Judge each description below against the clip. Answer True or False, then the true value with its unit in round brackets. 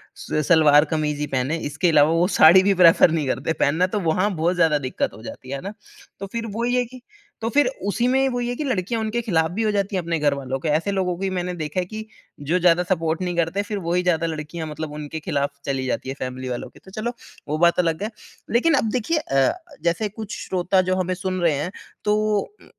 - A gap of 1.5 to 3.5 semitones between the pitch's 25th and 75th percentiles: False (5.1 semitones)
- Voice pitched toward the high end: False (175 Hz)